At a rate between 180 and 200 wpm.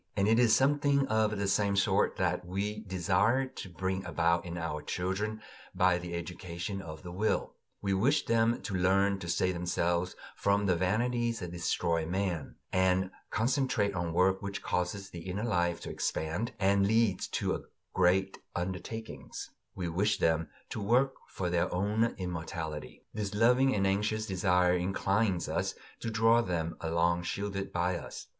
No: average, 160 wpm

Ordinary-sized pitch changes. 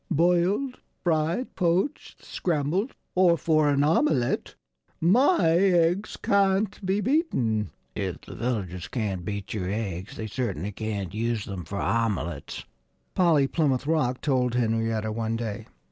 No: wide, 8.2 semitones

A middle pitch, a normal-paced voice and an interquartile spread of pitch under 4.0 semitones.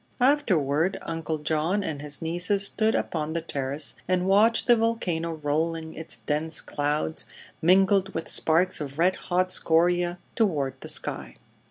Yes: medium, 165 Hz; average, 145 wpm; average, 3.4 semitones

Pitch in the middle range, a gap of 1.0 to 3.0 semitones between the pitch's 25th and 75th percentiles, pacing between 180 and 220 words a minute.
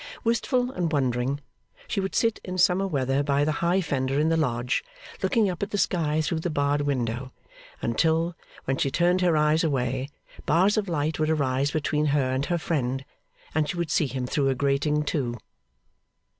No: medium, 150 Hz; average, 4.2 semitones; average, 185 wpm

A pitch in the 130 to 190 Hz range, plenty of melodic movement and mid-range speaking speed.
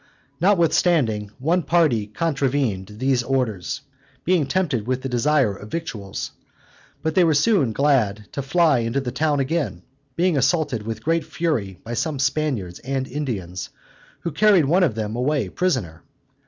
Yes: low, 135 Hz; wide, 6.0 semitones; average, 150 wpm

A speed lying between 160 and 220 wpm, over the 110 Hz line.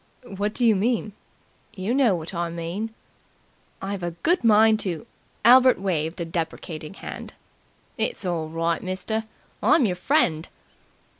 No: average, 145 wpm; high, 190 Hz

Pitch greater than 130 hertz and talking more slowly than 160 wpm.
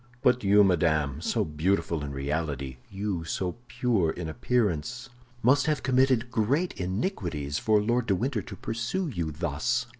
No: low, 100 Hz; average, 150 wpm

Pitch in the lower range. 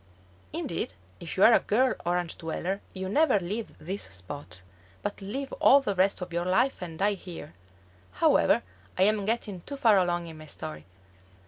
No: medium, 185 Hz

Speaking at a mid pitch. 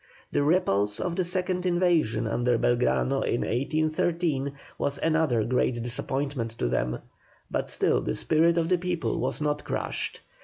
Yes: medium, 145 Hz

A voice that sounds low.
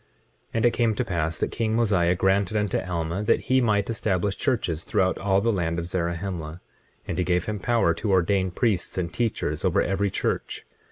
Yes: very low, 95 Hz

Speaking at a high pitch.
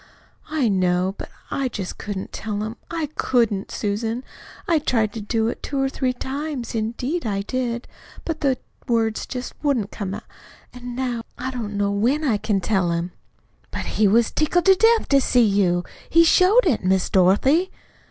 Yes: high, 235 Hz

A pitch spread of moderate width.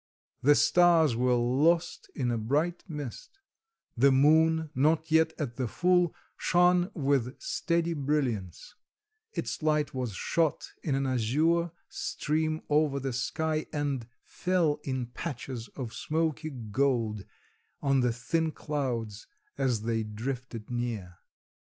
Yes: average, 4.7 semitones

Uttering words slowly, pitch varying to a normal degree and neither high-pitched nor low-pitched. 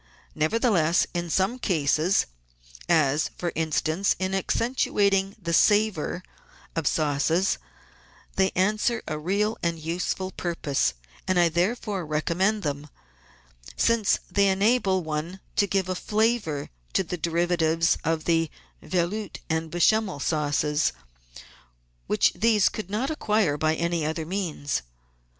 Yes: slow, 125 wpm; average, 4.1 semitones; medium, 175 Hz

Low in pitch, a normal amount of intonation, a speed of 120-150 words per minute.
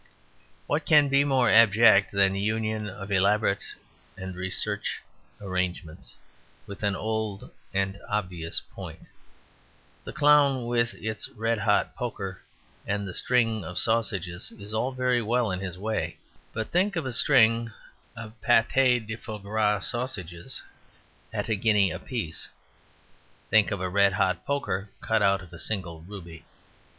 Yes: low, 105 Hz; average, 3.3 semitones; average, 145 wpm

